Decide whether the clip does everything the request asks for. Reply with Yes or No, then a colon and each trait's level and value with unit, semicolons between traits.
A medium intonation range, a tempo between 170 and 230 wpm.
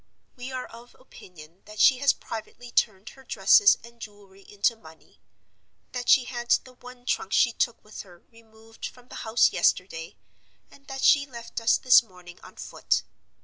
Yes: average, 3.7 semitones; average, 175 wpm